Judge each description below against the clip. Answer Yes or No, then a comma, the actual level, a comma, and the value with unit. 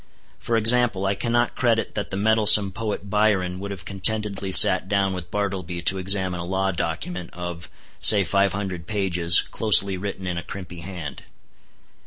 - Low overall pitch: Yes, very low, 95 Hz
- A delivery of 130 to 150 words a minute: No, average, 165 wpm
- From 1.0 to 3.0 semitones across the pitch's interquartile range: Yes, narrow, 2.4 semitones